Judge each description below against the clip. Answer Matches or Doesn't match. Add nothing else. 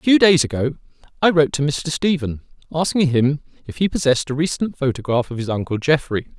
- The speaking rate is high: Doesn't match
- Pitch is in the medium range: Matches